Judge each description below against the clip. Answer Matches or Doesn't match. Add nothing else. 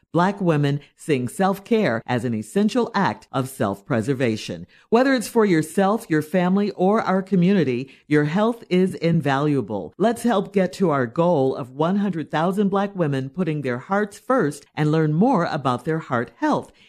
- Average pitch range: Doesn't match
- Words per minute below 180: Matches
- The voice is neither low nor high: Matches